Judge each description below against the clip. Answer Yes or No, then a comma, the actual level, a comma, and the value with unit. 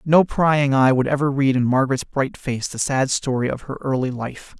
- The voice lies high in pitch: No, low, 135 Hz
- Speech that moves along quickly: Yes, fast, 220 wpm